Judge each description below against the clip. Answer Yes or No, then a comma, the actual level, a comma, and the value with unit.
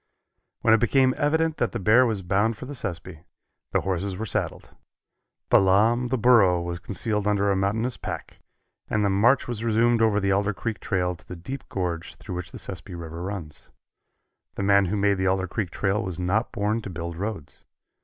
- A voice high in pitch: No, low, 100 Hz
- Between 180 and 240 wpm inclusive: Yes, average, 195 wpm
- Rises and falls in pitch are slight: No, average, 3.6 semitones